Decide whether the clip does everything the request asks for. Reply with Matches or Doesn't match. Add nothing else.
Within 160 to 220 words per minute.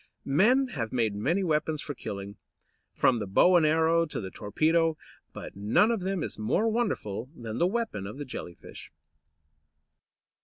Matches